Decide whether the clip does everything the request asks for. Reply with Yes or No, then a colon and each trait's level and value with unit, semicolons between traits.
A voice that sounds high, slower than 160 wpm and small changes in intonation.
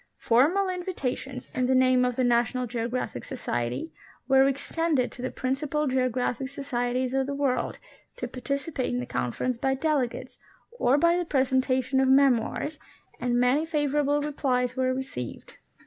Yes: very high, 260 Hz; average, 150 wpm; narrow, 2.3 semitones